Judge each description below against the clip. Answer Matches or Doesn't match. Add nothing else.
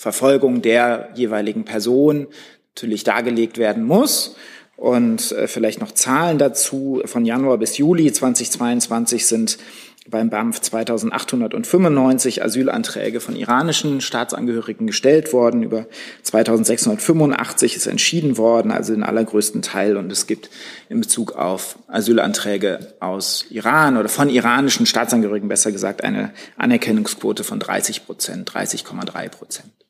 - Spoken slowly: Matches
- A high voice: Doesn't match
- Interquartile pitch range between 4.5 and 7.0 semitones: Matches